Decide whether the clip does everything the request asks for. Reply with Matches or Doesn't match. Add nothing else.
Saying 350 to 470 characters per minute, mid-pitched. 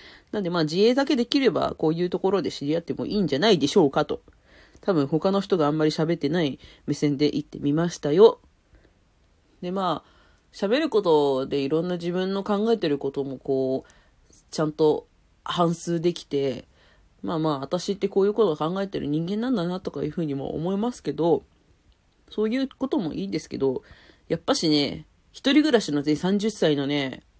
Matches